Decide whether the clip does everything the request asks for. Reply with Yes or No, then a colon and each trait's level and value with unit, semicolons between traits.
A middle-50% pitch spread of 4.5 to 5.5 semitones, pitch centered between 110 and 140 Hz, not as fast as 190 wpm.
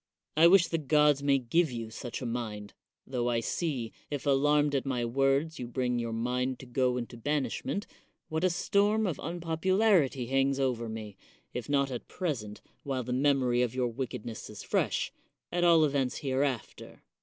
No: average, 3.7 semitones; low, 135 Hz; average, 180 wpm